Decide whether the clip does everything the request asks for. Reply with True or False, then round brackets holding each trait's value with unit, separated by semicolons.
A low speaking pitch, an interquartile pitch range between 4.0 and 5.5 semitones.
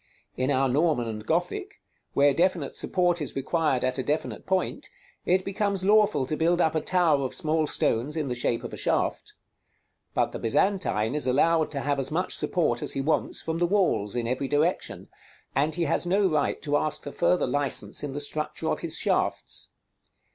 False (155 Hz; 4.5 semitones)